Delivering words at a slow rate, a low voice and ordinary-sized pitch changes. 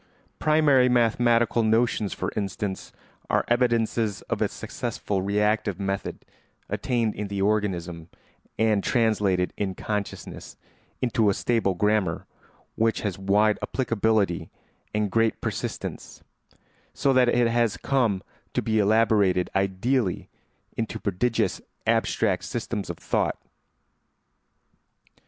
Yes: slow, 110 wpm; low, 110 Hz; average, 3.0 semitones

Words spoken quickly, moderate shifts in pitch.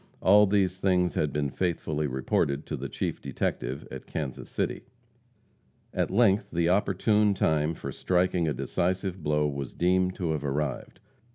No: average, 155 wpm; average, 4.0 semitones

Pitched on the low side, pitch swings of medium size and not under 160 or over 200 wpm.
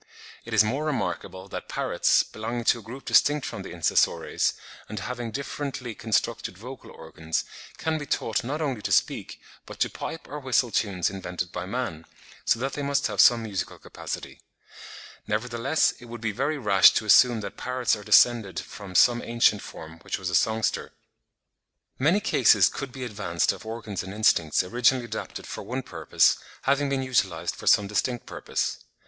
Yes: low, 115 Hz; average, 4.5 semitones; average, 175 wpm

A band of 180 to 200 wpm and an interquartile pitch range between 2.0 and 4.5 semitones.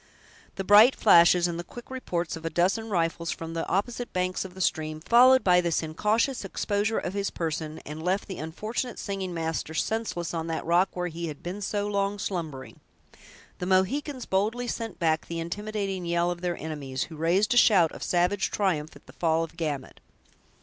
Yes: average, 190 wpm; average, 3.9 semitones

